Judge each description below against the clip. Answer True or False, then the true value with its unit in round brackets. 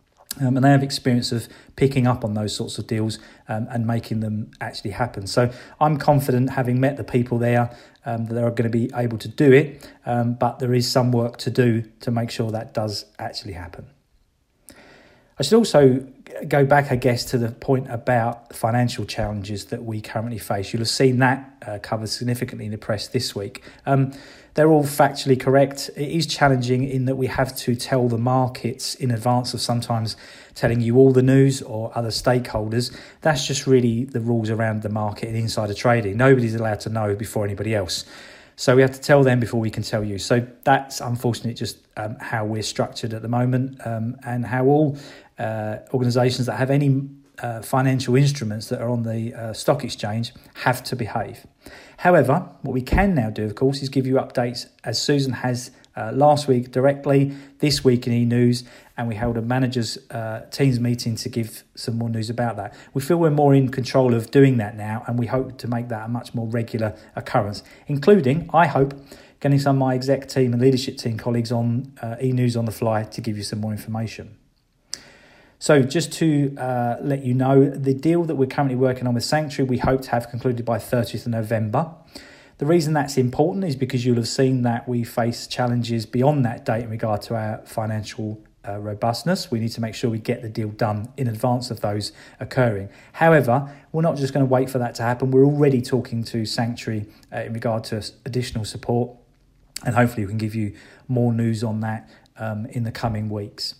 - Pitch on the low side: True (120 Hz)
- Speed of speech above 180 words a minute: True (205 wpm)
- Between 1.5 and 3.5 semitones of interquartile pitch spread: True (2.8 semitones)